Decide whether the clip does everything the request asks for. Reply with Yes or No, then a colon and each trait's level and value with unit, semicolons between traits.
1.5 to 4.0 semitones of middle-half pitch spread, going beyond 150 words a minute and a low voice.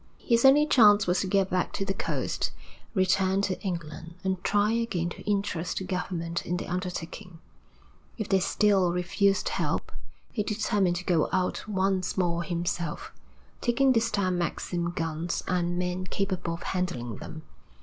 No: narrow, 2.4 semitones; average, 160 wpm; medium, 185 Hz